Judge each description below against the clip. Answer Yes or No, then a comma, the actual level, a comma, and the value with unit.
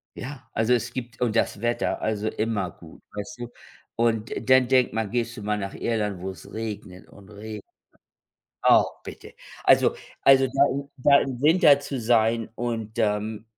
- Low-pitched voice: Yes, low, 115 Hz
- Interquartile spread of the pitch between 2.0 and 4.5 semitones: Yes, average, 2.8 semitones